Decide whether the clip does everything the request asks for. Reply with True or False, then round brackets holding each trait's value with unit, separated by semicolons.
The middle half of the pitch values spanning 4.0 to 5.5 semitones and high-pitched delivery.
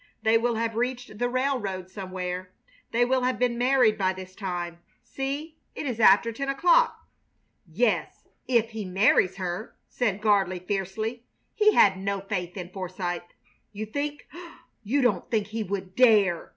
True (4.7 semitones; 215 Hz)